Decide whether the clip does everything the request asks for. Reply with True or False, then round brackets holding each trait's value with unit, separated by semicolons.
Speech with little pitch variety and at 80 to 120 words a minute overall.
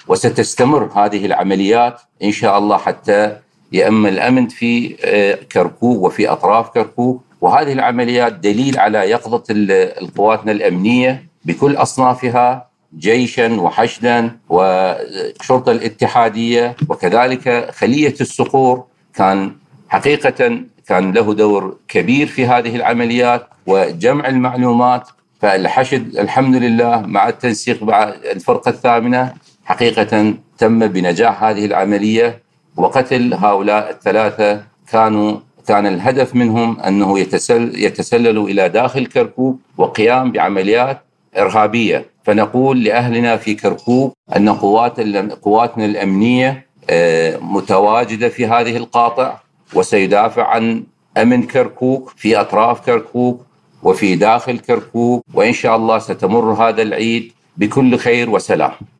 False (3.0 semitones; 105 wpm)